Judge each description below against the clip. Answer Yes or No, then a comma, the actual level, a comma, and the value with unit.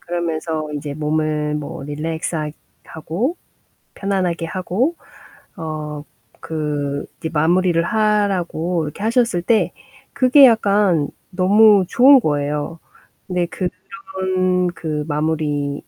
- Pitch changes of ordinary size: Yes, average, 4.3 semitones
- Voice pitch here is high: No, medium, 170 Hz